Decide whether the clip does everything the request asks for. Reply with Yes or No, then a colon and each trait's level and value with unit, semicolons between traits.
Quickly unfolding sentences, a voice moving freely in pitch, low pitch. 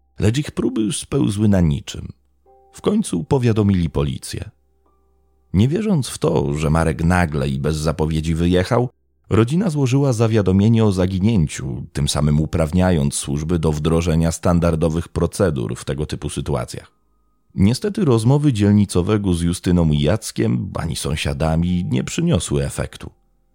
No: average, 125 wpm; wide, 6.6 semitones; very low, 85 Hz